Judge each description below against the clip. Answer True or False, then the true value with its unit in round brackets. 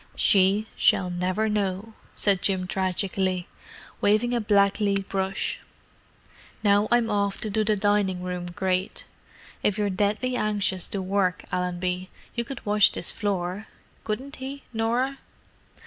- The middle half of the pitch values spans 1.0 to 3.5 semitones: True (2.4 semitones)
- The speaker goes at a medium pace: False (130 wpm)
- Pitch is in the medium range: False (200 Hz)